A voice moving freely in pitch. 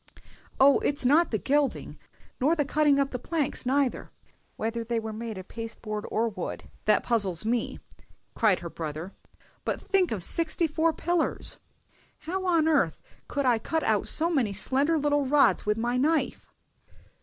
Yes: wide, 5.7 semitones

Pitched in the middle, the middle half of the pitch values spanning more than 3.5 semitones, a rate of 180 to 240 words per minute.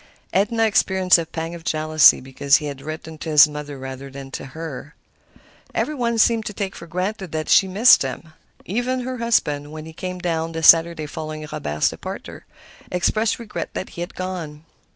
Yes: medium, 165 Hz; average, 4.3 semitones; average, 185 wpm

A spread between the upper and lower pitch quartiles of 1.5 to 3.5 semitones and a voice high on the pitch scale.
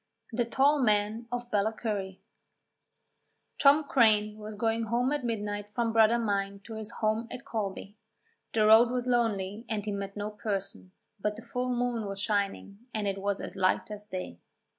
Yes: narrow, 2.6 semitones; high, 215 Hz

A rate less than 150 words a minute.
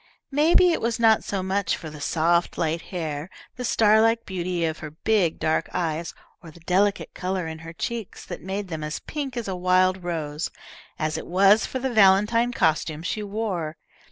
No: average, 190 wpm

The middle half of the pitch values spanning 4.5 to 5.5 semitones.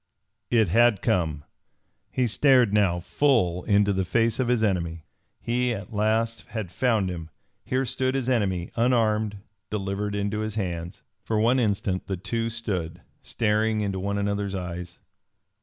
No: average, 3.5 semitones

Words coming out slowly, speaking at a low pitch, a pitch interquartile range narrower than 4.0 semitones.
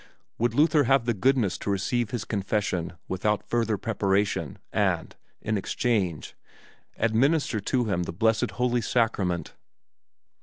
Yes: slow, 125 wpm; low, 110 Hz; average, 3.6 semitones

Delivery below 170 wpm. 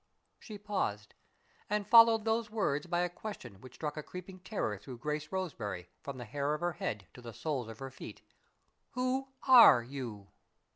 No: average, 185 wpm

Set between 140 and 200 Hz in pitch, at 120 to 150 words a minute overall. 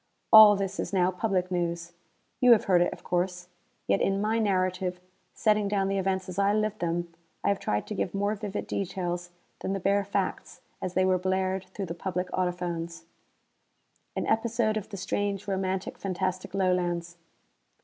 No: high, 190 Hz; average, 175 wpm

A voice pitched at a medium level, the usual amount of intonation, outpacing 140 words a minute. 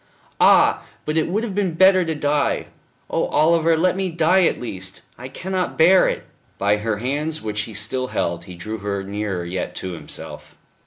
No: medium, 145 Hz; wide, 8.7 semitones; average, 190 wpm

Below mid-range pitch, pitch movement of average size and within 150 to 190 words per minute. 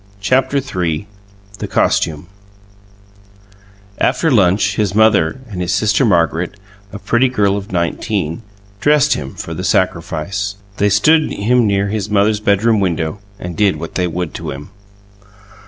No: low, 100 Hz; average, 3.6 semitones; average, 140 wpm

